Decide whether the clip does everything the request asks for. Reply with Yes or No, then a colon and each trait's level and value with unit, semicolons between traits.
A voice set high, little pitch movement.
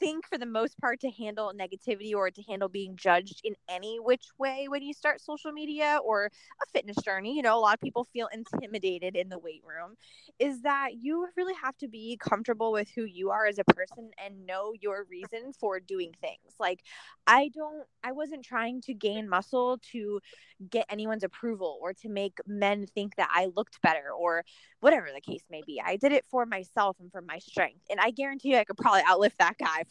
No: high, 220 Hz; average, 5.1 semitones